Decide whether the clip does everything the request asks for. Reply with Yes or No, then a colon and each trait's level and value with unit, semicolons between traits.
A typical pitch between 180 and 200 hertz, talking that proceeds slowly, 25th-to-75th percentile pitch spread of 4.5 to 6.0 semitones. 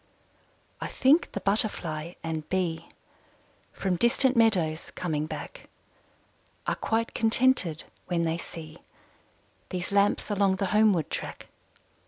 Yes: medium, 185 Hz; slow, 115 wpm; average, 4.9 semitones